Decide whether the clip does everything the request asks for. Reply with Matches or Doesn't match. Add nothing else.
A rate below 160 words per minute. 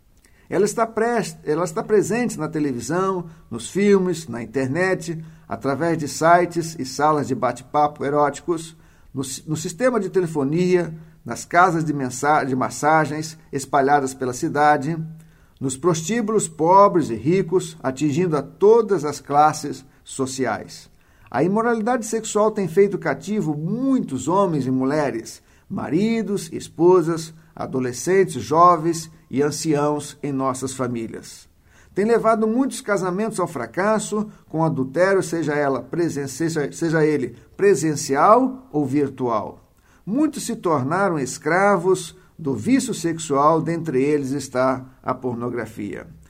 Matches